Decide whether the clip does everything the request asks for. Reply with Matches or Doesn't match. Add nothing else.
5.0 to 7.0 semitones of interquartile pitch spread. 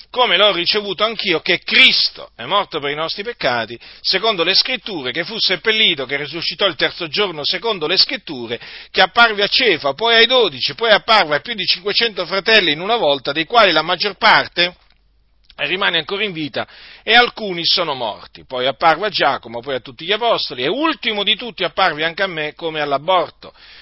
Matches